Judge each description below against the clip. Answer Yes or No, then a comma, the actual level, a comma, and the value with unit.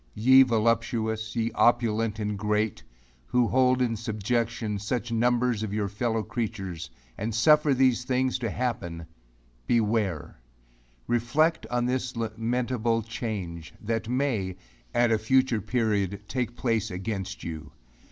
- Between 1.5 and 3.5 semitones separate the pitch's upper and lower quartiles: Yes, narrow, 2.6 semitones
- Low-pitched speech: Yes, low, 115 Hz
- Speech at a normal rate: No, slow, 125 wpm